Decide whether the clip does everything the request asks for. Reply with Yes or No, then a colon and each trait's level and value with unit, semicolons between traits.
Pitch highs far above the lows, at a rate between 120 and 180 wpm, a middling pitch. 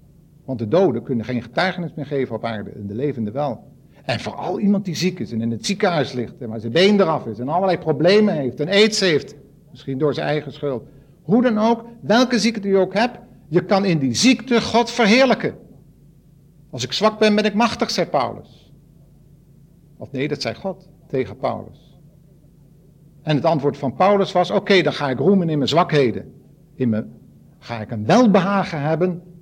No: wide, 5.7 semitones; average, 195 wpm; medium, 155 Hz